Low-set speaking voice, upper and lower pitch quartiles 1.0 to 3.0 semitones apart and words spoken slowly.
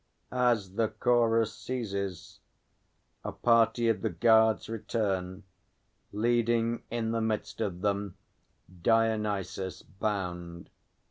Yes: low, 110 Hz; narrow, 2.6 semitones; slow, 95 wpm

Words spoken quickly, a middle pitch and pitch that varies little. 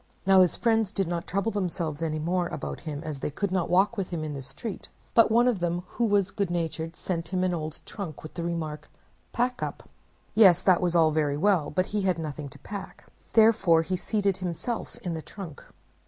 No: fast, 215 wpm; medium, 180 Hz; average, 3.7 semitones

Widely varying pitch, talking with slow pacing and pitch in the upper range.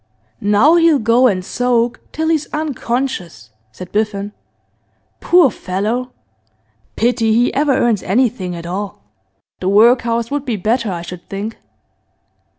No: average, 4.4 semitones; slow, 130 wpm; high, 230 Hz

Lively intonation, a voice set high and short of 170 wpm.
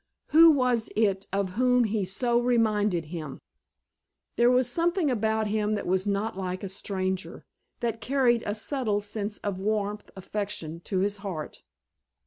No: average, 3.6 semitones; high, 210 Hz; average, 150 wpm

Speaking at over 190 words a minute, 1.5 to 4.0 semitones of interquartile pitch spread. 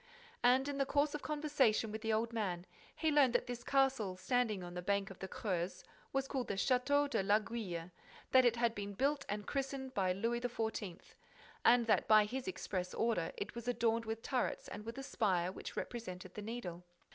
No: average, 200 wpm; average, 4.7 semitones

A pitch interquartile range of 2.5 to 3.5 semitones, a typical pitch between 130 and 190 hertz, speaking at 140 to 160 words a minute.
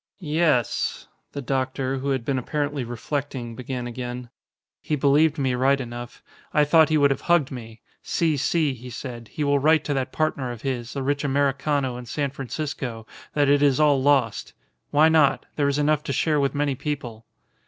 No: average, 2.8 semitones; medium, 140 Hz; average, 185 wpm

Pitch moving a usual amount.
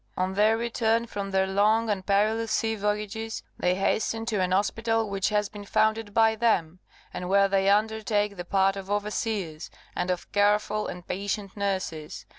No: narrow, 2.3 semitones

